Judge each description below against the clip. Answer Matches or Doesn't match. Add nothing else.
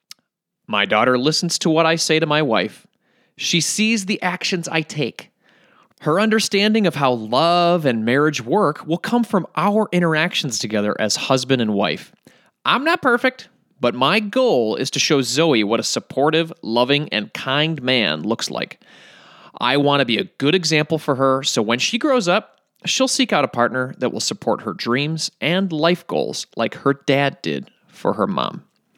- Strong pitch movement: Matches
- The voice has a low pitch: Doesn't match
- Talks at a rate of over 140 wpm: Matches